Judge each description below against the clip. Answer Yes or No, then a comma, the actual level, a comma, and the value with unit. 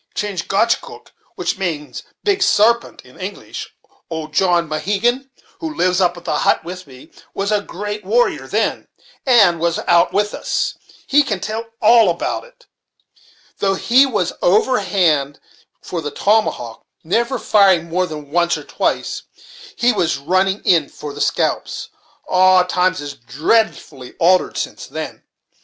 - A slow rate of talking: No, average, 150 wpm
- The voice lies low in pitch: No, medium, 185 Hz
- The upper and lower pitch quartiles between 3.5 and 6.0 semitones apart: Yes, average, 4.5 semitones